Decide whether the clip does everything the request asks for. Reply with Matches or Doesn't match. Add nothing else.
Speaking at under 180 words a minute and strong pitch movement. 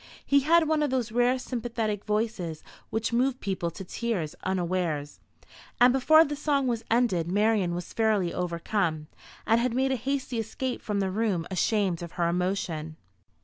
Matches